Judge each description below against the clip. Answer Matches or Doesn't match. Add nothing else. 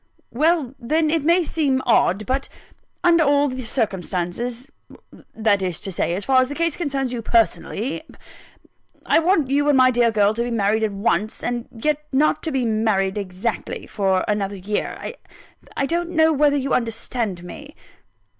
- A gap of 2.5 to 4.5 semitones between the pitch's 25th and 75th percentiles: Doesn't match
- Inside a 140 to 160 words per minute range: Doesn't match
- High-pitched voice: Matches